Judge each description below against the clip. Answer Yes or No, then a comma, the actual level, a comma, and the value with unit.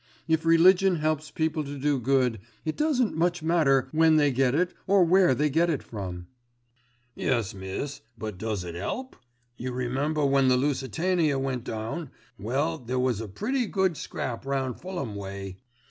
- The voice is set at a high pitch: No, medium, 140 Hz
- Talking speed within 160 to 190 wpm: Yes, average, 165 wpm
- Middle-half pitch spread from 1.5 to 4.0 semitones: No, average, 5.1 semitones